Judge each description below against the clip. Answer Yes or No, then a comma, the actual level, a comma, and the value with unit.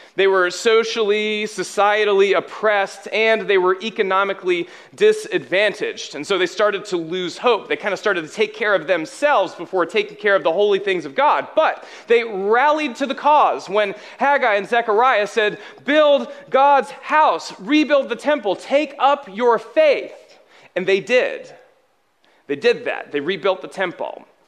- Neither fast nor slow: Yes, average, 160 wpm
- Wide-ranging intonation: Yes, wide, 7.1 semitones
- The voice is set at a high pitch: Yes, high, 230 Hz